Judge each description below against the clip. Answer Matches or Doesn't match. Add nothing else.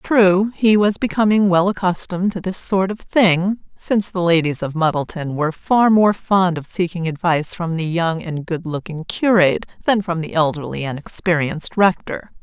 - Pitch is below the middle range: Doesn't match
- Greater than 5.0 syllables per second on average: Doesn't match